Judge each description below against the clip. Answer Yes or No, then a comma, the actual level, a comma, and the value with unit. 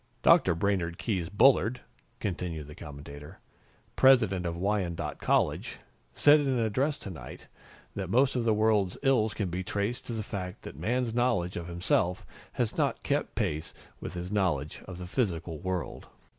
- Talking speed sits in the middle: Yes, average, 160 wpm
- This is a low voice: Yes, very low, 95 Hz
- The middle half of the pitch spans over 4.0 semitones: Yes, average, 4.7 semitones